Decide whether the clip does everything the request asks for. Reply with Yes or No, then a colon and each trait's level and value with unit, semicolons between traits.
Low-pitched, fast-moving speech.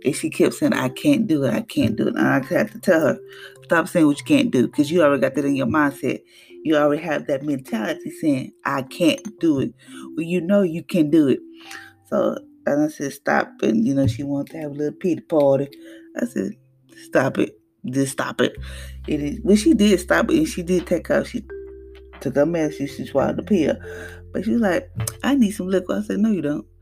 No: medium, 160 Hz; fast, 235 wpm